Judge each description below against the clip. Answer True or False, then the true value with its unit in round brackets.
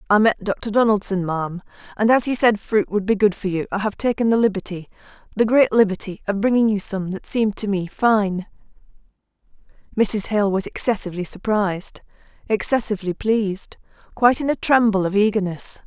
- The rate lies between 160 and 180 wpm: True (165 wpm)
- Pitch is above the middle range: True (205 Hz)